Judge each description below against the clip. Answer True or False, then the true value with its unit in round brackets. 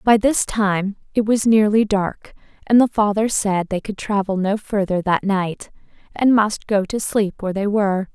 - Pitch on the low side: False (205 Hz)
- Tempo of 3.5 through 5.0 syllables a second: True (4.5 syllables/s)